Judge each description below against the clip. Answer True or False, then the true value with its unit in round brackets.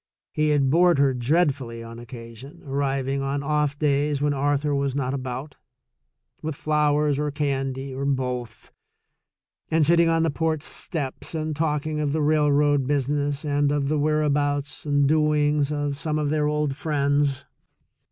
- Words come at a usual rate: True (150 wpm)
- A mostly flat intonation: True (1.6 semitones)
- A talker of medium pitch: True (145 Hz)